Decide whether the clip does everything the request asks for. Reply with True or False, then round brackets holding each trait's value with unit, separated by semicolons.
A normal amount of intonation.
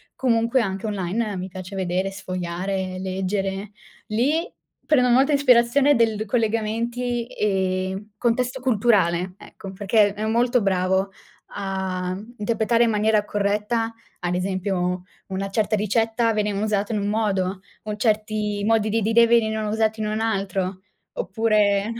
True (3.0 semitones)